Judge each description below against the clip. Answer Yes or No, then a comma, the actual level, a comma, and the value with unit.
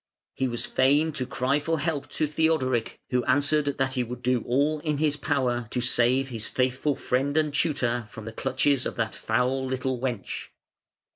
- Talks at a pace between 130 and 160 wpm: No, average, 185 wpm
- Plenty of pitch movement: No, average, 2.8 semitones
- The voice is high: No, low, 130 Hz